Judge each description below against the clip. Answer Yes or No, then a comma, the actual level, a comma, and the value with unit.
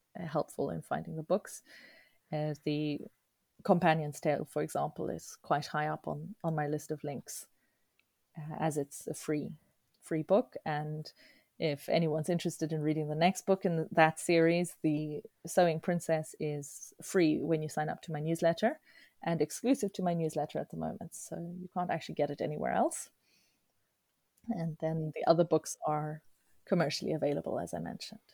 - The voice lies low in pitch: No, medium, 160 Hz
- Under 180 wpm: Yes, average, 165 wpm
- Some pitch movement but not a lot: No, narrow, 2.3 semitones